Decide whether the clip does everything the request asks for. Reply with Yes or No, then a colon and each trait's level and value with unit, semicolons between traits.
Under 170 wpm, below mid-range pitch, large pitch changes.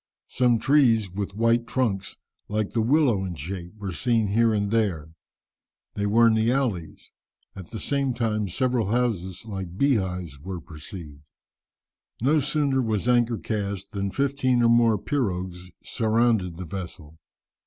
No: average, 145 wpm; low, 110 Hz; average, 4.3 semitones